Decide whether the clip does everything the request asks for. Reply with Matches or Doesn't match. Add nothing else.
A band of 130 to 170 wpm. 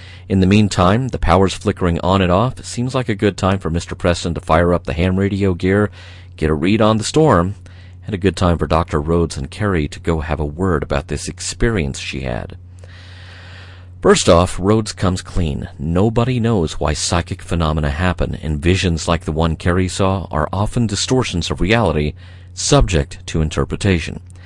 Doesn't match